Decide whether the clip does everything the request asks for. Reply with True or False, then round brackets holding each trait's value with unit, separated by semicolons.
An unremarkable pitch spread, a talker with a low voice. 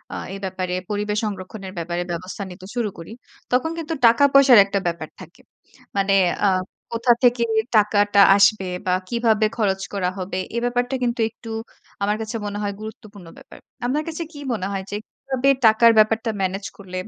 False (3.5 semitones; 210 Hz)